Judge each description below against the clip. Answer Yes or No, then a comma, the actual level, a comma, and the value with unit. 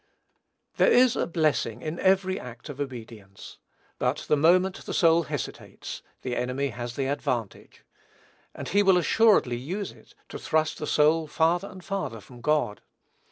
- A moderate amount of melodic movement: No, wide, 6.5 semitones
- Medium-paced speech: Yes, average, 160 wpm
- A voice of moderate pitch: Yes, medium, 150 Hz